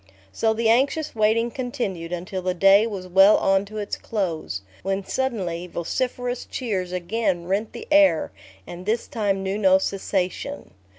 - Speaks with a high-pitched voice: Yes, high, 195 Hz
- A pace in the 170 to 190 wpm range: No, average, 155 wpm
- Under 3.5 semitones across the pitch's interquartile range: No, average, 3.9 semitones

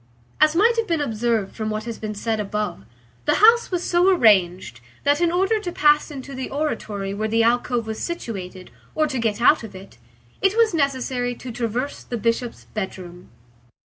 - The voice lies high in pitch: Yes, high, 240 Hz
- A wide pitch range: Yes, wide, 6.3 semitones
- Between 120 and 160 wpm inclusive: No, average, 185 wpm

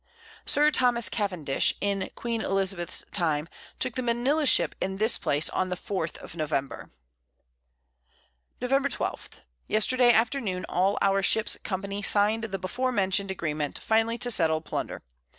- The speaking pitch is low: No, high, 200 Hz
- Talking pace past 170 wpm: No, average, 140 wpm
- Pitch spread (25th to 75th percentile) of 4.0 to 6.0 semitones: Yes, average, 4.6 semitones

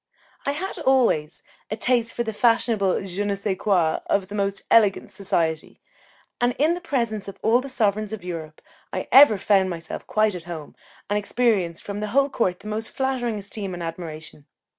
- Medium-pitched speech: No, high, 205 Hz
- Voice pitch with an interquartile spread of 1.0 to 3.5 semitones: No, average, 4.4 semitones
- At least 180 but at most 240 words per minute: Yes, average, 185 wpm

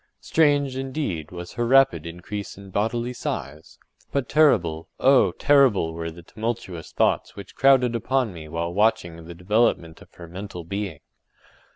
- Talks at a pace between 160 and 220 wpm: No, average, 145 wpm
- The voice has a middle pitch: No, low, 100 Hz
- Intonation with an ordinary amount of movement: No, wide, 7.0 semitones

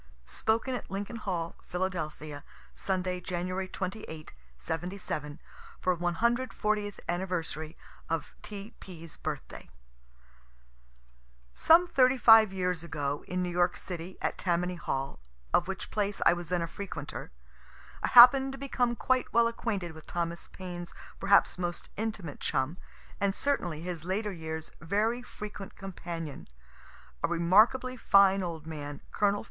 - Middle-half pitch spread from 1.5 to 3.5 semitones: No, average, 3.9 semitones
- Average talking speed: No, slow, 130 wpm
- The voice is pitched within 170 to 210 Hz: Yes, medium, 185 Hz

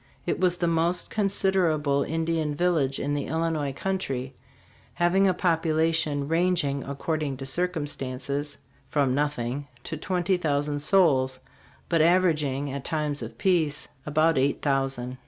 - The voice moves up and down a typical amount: Yes, average, 3.5 semitones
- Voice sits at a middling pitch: Yes, medium, 150 Hz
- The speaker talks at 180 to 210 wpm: No, slow, 135 wpm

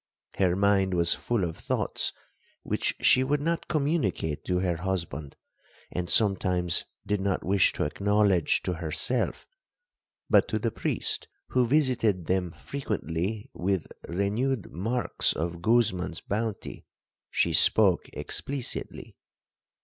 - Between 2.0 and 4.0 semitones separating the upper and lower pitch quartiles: No, average, 4.9 semitones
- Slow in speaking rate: Yes, slow, 120 wpm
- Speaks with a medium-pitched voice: No, very low, 95 Hz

